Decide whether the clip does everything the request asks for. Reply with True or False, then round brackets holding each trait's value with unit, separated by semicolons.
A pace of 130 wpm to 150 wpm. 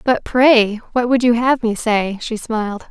False (205 wpm)